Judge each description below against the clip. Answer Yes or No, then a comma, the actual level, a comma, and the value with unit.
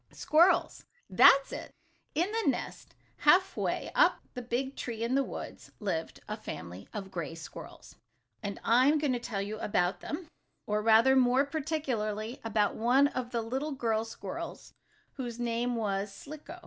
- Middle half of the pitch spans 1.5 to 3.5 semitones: No, average, 4.4 semitones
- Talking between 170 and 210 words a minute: No, average, 160 wpm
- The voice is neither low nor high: No, high, 240 Hz